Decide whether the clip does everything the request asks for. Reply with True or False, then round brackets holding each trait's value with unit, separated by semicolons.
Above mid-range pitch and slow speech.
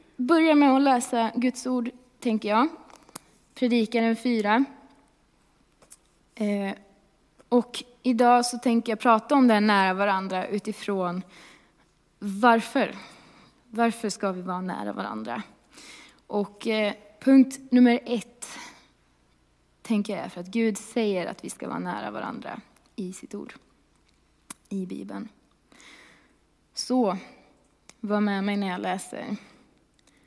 True (225 Hz; 115 wpm)